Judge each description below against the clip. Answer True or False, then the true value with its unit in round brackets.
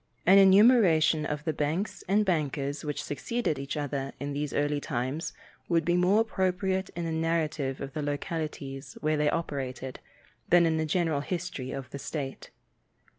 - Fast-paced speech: False (165 wpm)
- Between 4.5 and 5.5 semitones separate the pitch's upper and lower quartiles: False (3.7 semitones)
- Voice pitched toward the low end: False (155 Hz)